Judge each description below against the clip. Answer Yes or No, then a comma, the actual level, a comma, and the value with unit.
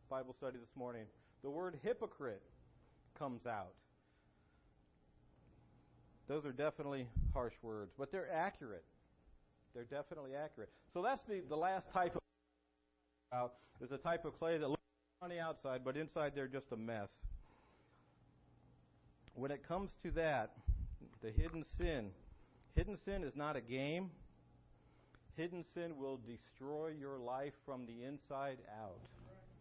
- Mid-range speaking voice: No, low, 130 Hz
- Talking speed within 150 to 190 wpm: No, slow, 135 wpm